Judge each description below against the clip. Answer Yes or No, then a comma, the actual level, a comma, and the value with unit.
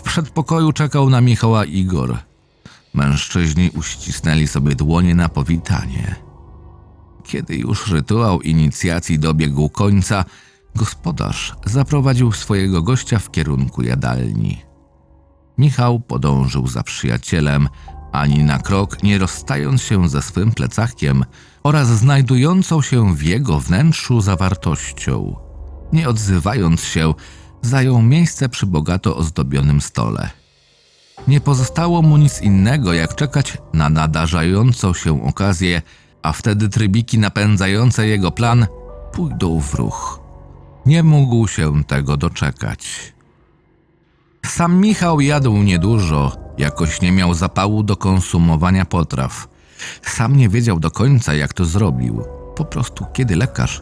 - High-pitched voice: No, very low, 90 Hz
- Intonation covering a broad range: Yes, wide, 7.7 semitones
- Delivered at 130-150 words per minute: No, average, 115 wpm